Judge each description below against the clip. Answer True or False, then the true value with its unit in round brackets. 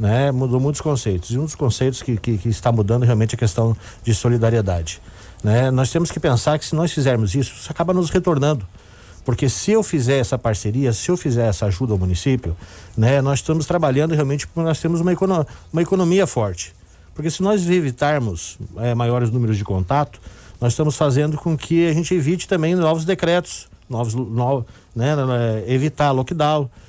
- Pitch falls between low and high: False (130 Hz)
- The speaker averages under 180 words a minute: False (185 wpm)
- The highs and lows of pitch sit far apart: True (5.9 semitones)